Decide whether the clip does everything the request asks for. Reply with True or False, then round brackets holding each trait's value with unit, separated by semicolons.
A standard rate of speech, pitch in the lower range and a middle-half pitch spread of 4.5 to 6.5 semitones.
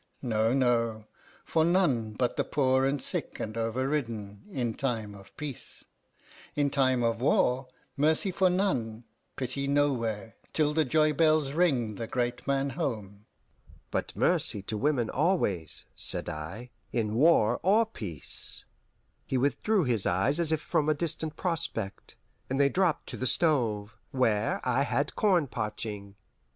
True (145 wpm; 130 Hz; 5.3 semitones)